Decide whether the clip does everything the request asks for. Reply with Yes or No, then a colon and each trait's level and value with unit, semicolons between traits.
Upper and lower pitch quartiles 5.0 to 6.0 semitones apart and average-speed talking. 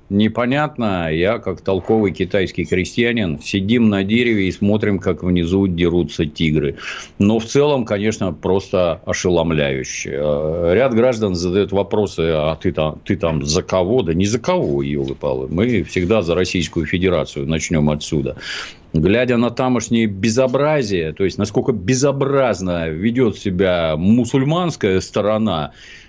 Yes: wide, 5.6 semitones; average, 130 wpm